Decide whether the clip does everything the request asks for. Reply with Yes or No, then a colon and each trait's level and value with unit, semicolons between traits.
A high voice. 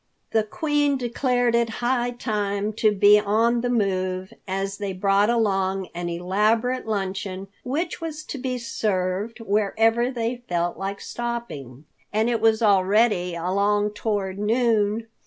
Yes: high, 210 Hz